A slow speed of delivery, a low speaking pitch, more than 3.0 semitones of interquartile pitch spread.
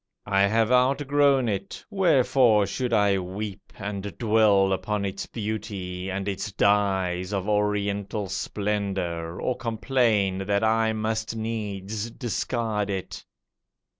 No: slow, 120 wpm; low, 105 Hz; narrow, 2.4 semitones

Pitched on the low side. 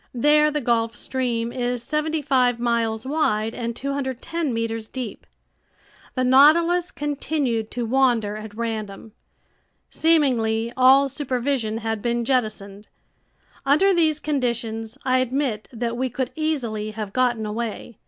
No: high, 245 Hz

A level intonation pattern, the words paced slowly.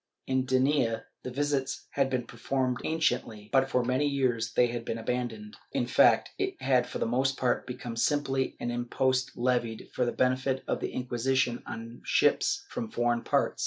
No: narrow, 1.9 semitones; average, 175 wpm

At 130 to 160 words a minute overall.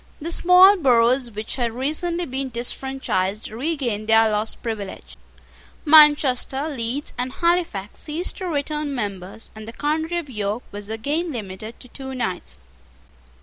Yes: average, 140 wpm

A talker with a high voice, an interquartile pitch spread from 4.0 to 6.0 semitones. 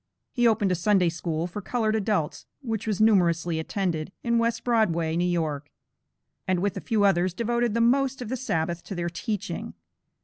Yes: high, 195 Hz; average, 4.8 semitones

